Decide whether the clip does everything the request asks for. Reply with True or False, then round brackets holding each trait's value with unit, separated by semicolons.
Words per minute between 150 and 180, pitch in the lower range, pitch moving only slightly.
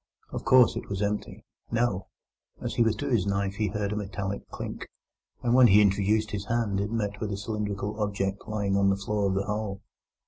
False (205 wpm; 105 Hz; 1.6 semitones)